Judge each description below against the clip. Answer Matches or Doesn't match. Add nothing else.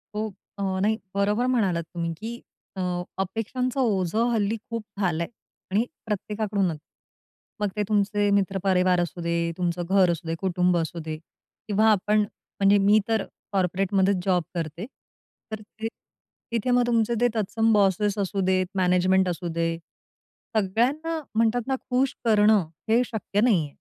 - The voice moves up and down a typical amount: Matches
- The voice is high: Matches